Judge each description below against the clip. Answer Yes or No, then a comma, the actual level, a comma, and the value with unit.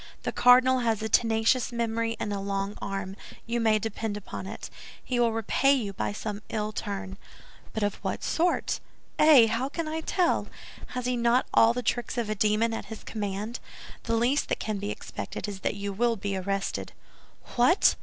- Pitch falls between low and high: No, high, 225 Hz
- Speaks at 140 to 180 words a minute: No, average, 190 wpm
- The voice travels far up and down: No, average, 3.0 semitones